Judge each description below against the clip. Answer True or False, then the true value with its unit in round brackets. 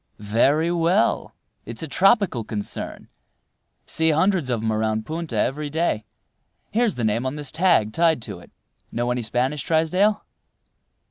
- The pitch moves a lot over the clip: True (6.6 semitones)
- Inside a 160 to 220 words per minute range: False (145 wpm)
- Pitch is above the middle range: False (145 Hz)